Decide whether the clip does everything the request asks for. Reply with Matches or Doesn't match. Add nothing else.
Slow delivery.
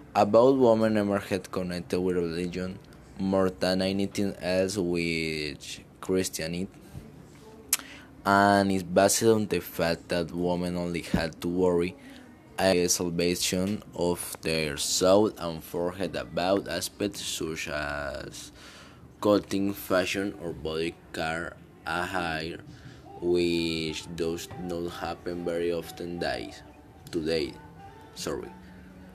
Matches